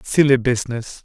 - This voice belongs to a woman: No, male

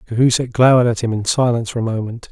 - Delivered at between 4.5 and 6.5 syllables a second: No, 7.3 syllables/s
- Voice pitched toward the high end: No, low, 115 Hz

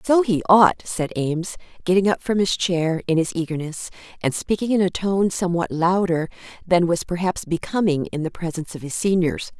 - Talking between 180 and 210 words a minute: Yes, average, 190 wpm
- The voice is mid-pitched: Yes, medium, 180 Hz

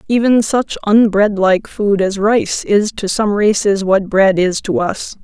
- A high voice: Yes, high, 205 Hz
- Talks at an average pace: Yes, average, 170 wpm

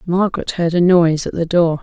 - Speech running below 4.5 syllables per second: No, 5.9 syllables/s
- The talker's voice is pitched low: No, medium, 170 Hz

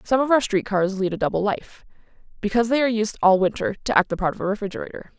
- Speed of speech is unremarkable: No, fast, 255 wpm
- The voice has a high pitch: Yes, high, 205 Hz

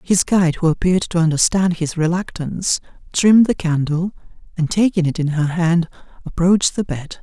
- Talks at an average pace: Yes, average, 165 wpm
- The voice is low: No, medium, 170 Hz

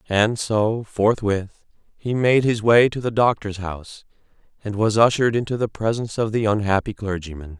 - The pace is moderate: Yes, average, 165 wpm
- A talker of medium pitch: No, low, 110 Hz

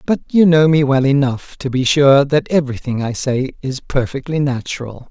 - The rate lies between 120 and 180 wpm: No, average, 200 wpm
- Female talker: No, male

